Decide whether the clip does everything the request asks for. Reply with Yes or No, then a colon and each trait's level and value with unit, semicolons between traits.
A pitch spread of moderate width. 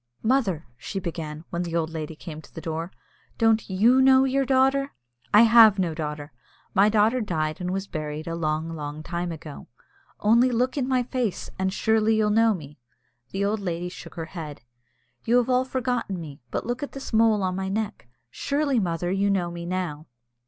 No: wide, 5.9 semitones